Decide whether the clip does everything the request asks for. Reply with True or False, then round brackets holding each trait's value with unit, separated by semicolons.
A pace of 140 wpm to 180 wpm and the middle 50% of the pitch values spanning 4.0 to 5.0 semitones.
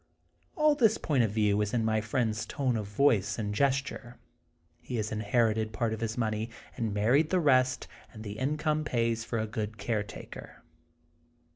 False (170 wpm; 3.4 semitones)